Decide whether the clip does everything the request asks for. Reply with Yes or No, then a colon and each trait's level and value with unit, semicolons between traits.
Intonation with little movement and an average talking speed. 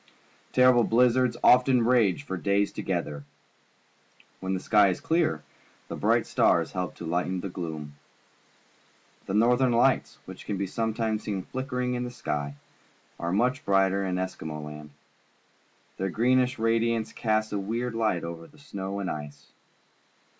No: average, 5.1 semitones; average, 145 wpm